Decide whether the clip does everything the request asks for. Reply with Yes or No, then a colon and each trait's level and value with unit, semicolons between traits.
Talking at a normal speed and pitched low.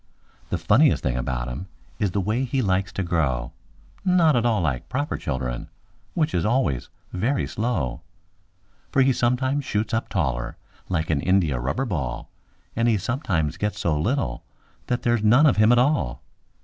Yes: average, 170 wpm; low, 100 Hz